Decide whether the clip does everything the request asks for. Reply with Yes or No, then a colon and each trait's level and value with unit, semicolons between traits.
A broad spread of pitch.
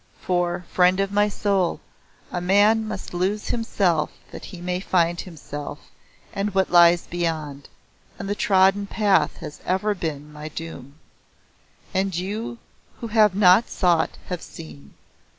No: average, 3.2 semitones